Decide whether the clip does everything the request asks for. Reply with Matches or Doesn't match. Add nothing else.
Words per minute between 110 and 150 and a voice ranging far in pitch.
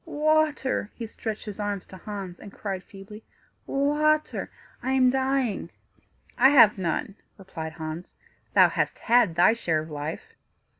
Matches